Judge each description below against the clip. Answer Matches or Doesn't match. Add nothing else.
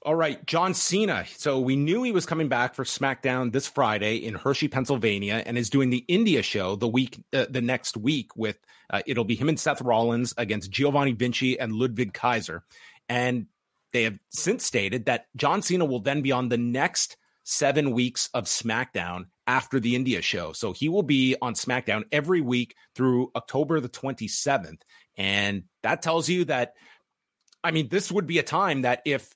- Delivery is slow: Doesn't match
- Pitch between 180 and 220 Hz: Doesn't match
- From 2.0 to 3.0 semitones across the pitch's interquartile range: Doesn't match